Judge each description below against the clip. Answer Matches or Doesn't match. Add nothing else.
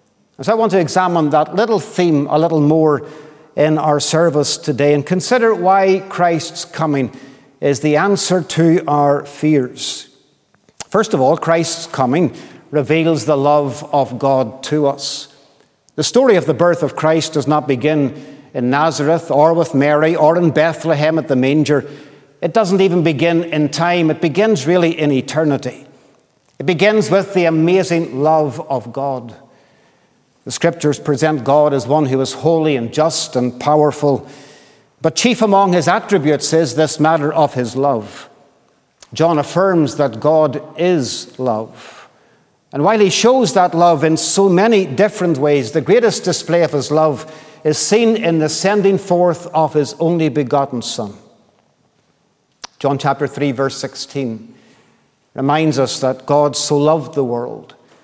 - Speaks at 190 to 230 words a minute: Doesn't match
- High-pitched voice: Doesn't match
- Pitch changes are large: Doesn't match